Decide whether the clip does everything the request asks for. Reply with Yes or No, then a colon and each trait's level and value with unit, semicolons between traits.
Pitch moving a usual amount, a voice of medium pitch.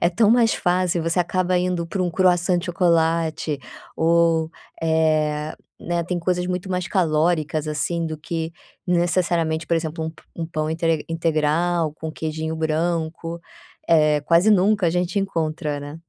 No: narrow, 2.0 semitones; medium, 165 Hz